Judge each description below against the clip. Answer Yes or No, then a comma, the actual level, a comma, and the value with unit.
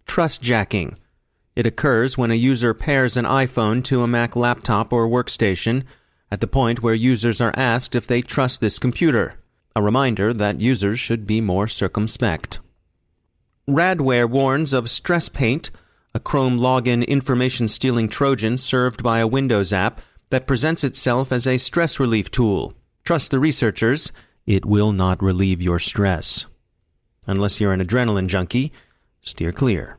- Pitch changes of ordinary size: Yes, average, 3.9 semitones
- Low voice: Yes, low, 115 Hz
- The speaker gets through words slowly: No, average, 150 wpm